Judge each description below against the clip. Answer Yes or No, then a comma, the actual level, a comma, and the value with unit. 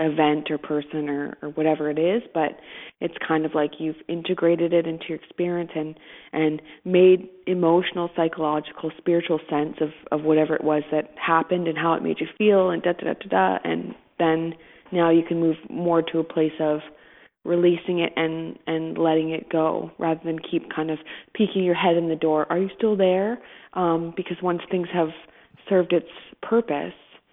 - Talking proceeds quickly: No, average, 190 wpm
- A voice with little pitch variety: Yes, narrow, 1.9 semitones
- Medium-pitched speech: Yes, medium, 165 Hz